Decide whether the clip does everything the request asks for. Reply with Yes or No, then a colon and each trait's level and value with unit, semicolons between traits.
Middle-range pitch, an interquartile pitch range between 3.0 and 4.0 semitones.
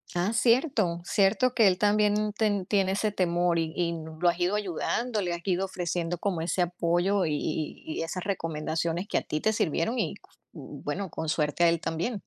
Yes: medium, 180 Hz; average, 3.5 semitones